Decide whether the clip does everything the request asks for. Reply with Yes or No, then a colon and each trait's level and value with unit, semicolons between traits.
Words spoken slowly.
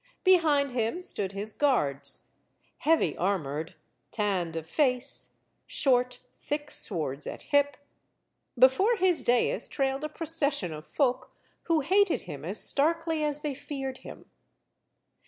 Yes: slow, 125 wpm